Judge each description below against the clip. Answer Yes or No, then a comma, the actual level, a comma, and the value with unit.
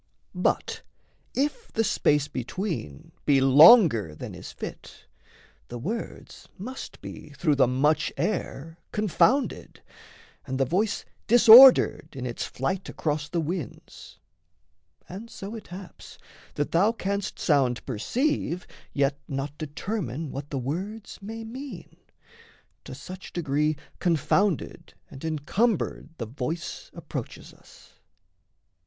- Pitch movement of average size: No, wide, 7.1 semitones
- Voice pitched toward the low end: No, medium, 165 Hz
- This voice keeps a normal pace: No, slow, 115 wpm